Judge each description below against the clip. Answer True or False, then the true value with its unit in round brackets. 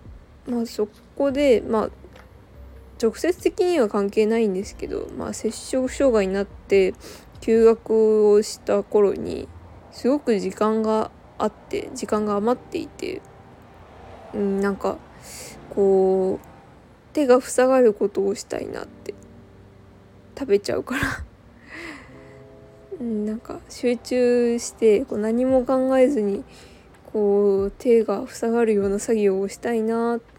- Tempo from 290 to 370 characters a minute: False (225 characters per minute)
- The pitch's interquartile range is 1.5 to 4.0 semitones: True (3.7 semitones)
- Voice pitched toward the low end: False (225 Hz)